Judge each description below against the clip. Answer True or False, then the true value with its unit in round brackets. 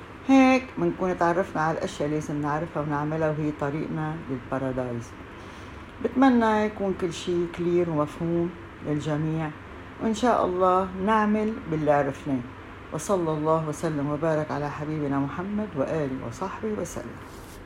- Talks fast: False (120 wpm)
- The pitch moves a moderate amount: True (4.2 semitones)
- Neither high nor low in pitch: True (155 Hz)